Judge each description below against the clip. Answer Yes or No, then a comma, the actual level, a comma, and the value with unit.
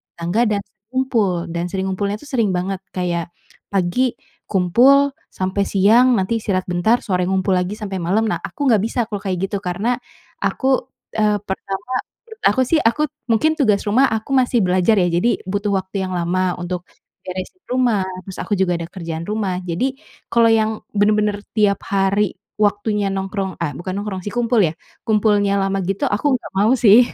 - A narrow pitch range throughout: No, average, 3.1 semitones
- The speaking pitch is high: Yes, high, 200 Hz